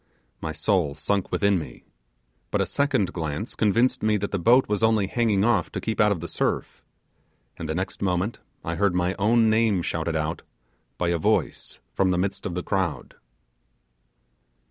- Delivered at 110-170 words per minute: No, average, 180 wpm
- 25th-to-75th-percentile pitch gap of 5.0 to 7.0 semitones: No, average, 4.0 semitones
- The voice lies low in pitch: Yes, very low, 95 Hz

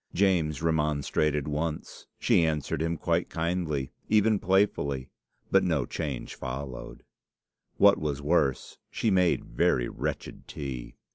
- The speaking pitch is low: Yes, very low, 75 Hz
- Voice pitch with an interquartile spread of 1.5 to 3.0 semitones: No, average, 3.5 semitones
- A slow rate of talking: Yes, slow, 120 wpm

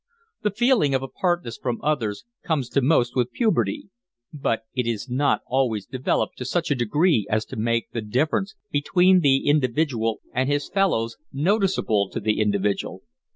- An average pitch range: No, wide, 6.1 semitones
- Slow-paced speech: No, average, 160 wpm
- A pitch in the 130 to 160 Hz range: Yes, low, 135 Hz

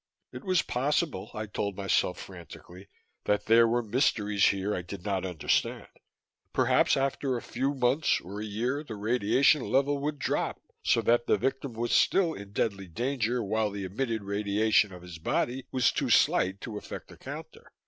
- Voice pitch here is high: No, low, 110 Hz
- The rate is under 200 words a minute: Yes, average, 180 wpm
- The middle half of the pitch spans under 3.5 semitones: No, average, 4.6 semitones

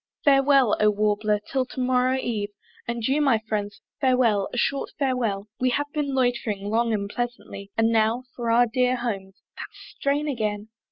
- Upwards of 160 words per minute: Yes, average, 170 wpm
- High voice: Yes, high, 235 Hz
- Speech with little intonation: No, average, 3.4 semitones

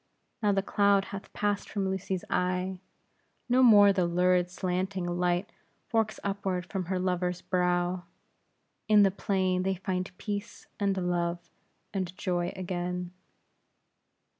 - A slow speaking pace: Yes, slow, 130 wpm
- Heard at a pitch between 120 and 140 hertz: No, medium, 185 Hz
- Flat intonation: Yes, narrow, 1.8 semitones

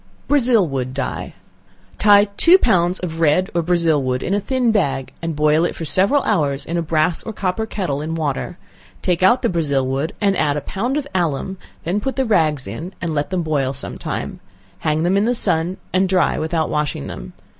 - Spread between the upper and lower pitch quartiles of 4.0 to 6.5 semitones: Yes, average, 4.7 semitones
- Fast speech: Yes, fast, 210 wpm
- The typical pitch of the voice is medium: Yes, medium, 170 Hz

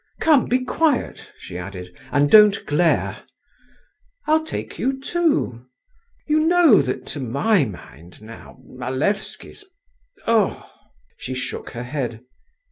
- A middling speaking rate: No, slow, 115 wpm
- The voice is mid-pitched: No, high, 195 Hz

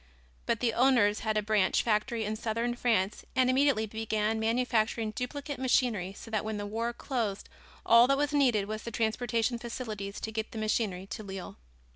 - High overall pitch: Yes, high, 225 Hz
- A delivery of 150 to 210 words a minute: Yes, average, 180 wpm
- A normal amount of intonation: No, narrow, 2.3 semitones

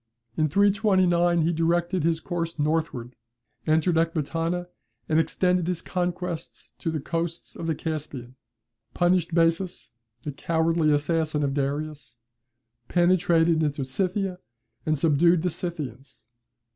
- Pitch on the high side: No, medium, 165 Hz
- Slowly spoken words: Yes, slow, 120 wpm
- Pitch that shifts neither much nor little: No, narrow, 2.2 semitones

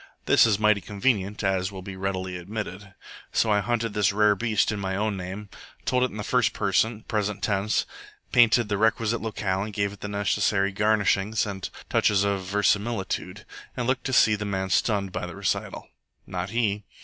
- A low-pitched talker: Yes, low, 105 Hz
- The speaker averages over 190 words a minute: No, average, 185 wpm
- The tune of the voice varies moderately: No, narrow, 1.9 semitones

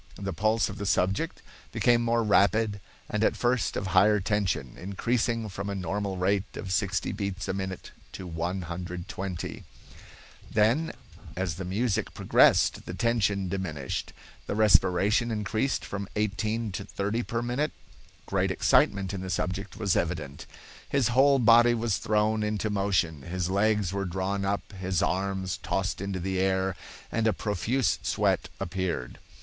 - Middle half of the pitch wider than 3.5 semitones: No, average, 2.7 semitones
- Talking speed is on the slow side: No, average, 150 wpm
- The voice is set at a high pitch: No, low, 100 Hz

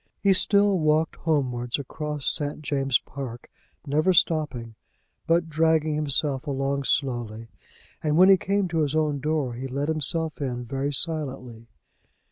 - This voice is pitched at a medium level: Yes, medium, 145 Hz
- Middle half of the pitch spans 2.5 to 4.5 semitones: Yes, average, 3.2 semitones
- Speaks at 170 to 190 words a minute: No, average, 140 wpm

